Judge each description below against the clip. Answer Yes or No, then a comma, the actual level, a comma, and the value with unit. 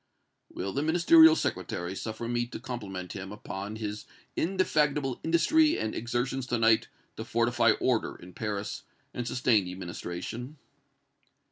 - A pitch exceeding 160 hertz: No, low, 120 Hz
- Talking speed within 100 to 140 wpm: Yes, slow, 135 wpm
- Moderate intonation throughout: No, wide, 6.0 semitones